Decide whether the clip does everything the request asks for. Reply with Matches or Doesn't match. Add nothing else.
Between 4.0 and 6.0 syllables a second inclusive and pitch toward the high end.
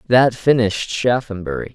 Doesn't match